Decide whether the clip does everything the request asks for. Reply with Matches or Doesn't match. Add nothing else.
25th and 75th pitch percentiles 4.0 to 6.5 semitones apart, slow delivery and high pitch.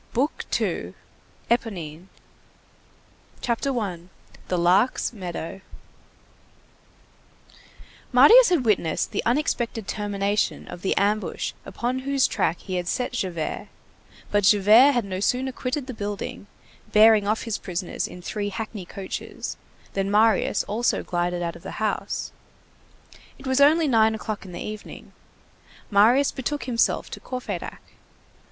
Matches